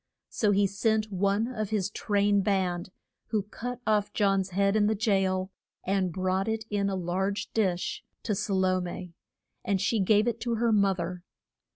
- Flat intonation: Yes, narrow, 2.3 semitones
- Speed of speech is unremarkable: Yes, average, 180 wpm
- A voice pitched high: Yes, high, 200 Hz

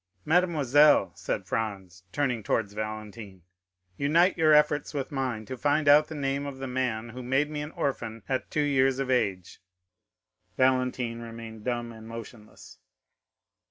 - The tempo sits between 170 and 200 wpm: No, average, 150 wpm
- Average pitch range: Yes, average, 4.4 semitones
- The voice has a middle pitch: No, low, 130 Hz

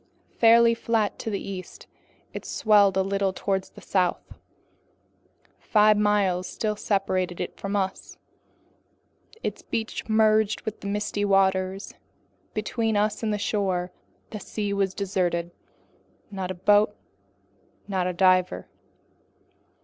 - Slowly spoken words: Yes, slow, 125 wpm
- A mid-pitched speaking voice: No, high, 200 Hz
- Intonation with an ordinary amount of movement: No, narrow, 2.1 semitones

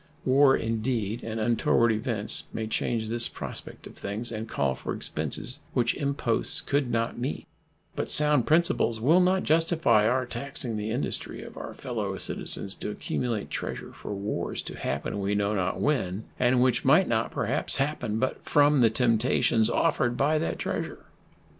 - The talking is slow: No, average, 165 wpm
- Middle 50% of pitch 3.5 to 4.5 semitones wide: Yes, average, 4.1 semitones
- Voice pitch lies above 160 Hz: No, low, 120 Hz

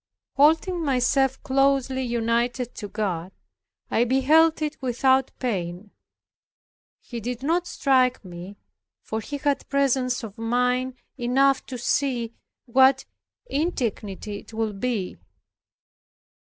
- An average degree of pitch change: Yes, average, 3.2 semitones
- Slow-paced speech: Yes, slow, 110 wpm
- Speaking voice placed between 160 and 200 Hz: No, very high, 250 Hz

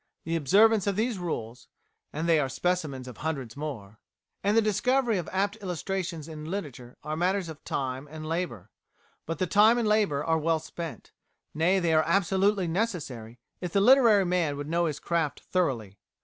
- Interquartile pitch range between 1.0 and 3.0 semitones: No, average, 5.0 semitones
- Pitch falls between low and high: Yes, medium, 165 Hz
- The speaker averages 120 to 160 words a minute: No, average, 175 wpm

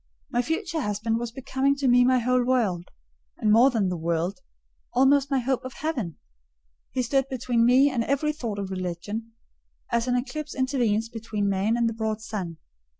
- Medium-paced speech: Yes, average, 180 wpm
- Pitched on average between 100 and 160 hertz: No, high, 240 Hz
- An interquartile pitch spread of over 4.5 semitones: No, average, 3.8 semitones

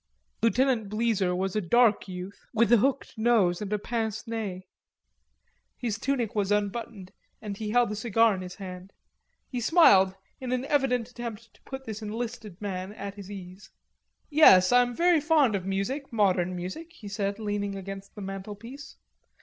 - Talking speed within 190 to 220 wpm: No, average, 165 wpm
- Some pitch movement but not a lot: Yes, average, 3.7 semitones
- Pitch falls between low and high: No, high, 215 Hz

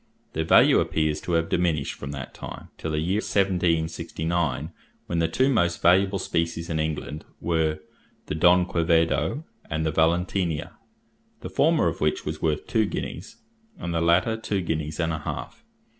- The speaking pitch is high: No, very low, 85 Hz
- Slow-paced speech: No, average, 165 wpm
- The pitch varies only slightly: Yes, narrow, 2.1 semitones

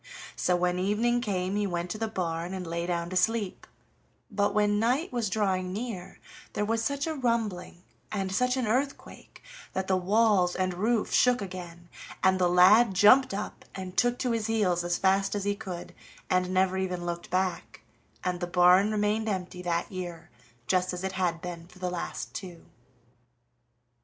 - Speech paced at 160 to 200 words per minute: Yes, average, 180 wpm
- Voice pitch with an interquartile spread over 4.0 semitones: No, average, 3.2 semitones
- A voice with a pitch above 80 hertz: Yes, high, 190 Hz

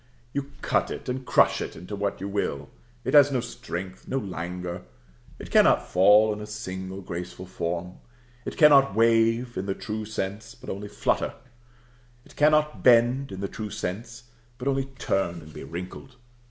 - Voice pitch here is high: No, low, 105 Hz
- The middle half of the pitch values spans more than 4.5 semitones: Yes, average, 4.9 semitones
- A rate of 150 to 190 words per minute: Yes, average, 170 wpm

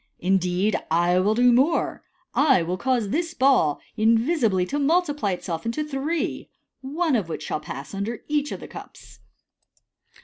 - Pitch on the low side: No, high, 230 Hz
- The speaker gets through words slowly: No, average, 160 wpm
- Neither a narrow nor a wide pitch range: No, wide, 7.9 semitones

